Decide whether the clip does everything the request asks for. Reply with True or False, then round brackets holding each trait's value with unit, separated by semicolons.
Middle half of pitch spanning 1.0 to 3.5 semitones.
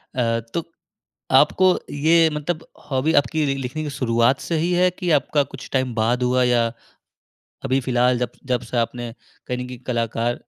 False (4.2 semitones)